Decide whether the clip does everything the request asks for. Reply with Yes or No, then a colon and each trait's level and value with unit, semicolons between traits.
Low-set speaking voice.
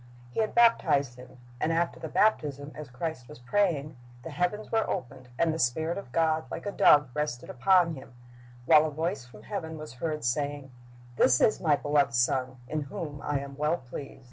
No: medium, 150 Hz